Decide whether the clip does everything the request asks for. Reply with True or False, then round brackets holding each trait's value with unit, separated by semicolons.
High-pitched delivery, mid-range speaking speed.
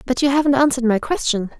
False (260 Hz; 225 wpm)